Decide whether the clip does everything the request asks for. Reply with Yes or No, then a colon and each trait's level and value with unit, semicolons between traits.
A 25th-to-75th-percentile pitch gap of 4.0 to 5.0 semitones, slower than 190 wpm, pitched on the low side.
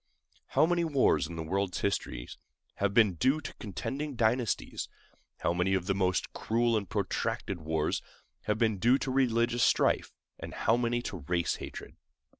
Yes: average, 4.6 semitones; average, 160 wpm; low, 110 Hz